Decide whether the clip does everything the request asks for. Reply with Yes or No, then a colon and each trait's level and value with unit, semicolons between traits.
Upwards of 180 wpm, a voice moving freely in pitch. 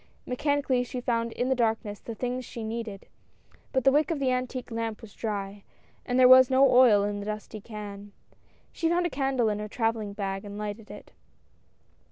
No: average, 195 wpm; average, 3.5 semitones